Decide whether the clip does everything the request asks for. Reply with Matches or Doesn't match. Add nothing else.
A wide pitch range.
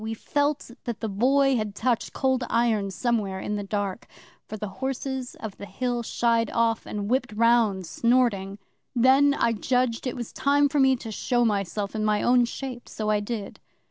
Doesn't match